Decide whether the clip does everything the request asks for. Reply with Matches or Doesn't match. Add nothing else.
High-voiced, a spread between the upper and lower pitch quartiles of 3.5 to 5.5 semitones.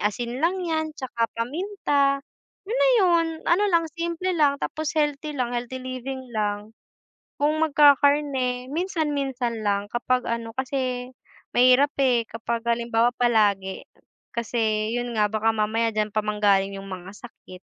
Matches